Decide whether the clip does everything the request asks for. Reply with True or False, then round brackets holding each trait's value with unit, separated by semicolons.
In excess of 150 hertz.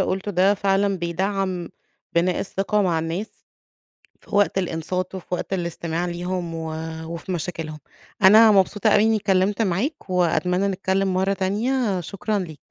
True (190 Hz)